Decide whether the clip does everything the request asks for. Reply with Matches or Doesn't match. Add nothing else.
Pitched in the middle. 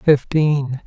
Matches